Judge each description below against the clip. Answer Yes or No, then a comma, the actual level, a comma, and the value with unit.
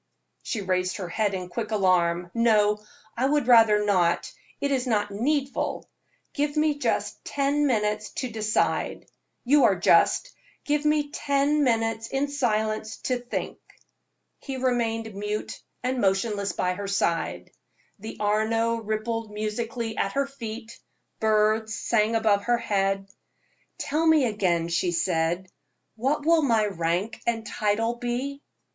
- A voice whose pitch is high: Yes, high, 220 Hz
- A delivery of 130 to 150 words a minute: Yes, average, 140 wpm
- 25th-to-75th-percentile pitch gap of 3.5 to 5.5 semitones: Yes, average, 3.8 semitones